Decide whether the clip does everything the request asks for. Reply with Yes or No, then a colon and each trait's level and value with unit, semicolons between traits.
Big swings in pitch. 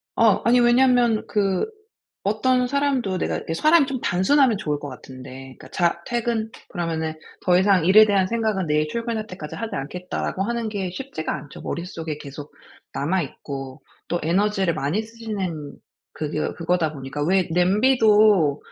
Yes: wide, 6.2 semitones